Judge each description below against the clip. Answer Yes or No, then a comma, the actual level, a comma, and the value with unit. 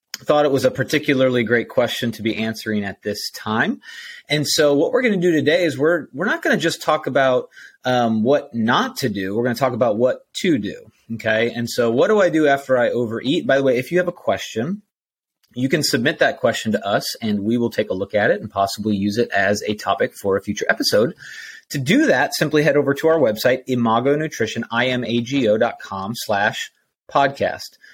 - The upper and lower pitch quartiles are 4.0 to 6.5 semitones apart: Yes, average, 4.7 semitones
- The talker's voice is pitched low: Yes, low, 125 Hz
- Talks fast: Yes, fast, 215 wpm